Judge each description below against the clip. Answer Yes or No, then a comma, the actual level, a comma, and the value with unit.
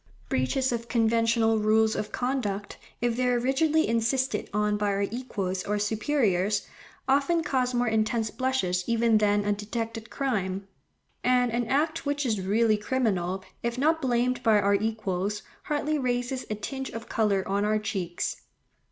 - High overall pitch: Yes, high, 225 Hz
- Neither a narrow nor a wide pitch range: Yes, average, 3.5 semitones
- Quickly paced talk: No, average, 155 wpm